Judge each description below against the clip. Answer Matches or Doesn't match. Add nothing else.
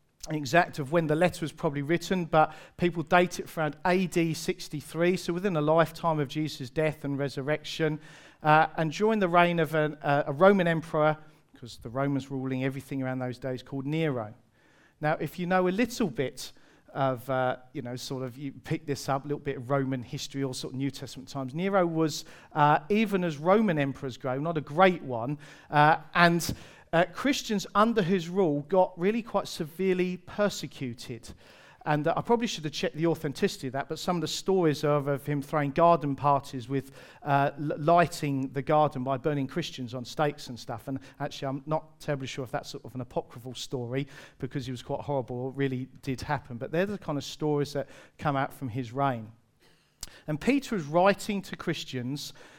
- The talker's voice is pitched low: Doesn't match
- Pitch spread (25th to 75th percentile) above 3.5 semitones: Matches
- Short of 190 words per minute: Doesn't match